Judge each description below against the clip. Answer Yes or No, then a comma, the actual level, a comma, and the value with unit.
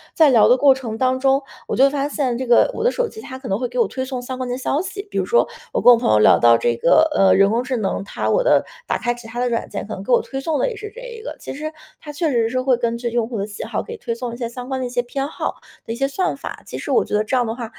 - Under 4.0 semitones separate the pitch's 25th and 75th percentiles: Yes, average, 3.5 semitones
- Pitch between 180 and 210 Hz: No, very high, 255 Hz